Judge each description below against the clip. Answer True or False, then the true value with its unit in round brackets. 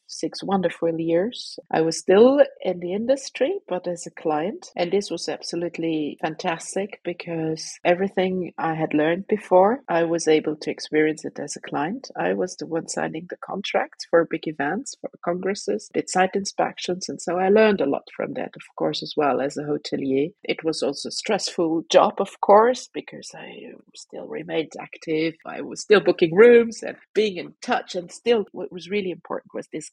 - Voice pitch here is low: False (180 Hz)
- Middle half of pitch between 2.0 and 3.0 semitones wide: False (3.8 semitones)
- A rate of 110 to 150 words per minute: False (185 wpm)